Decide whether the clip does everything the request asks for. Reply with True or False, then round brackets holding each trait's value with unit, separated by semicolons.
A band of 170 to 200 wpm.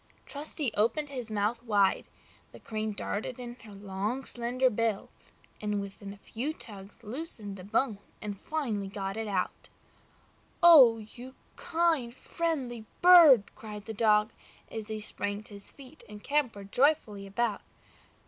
False (150 wpm)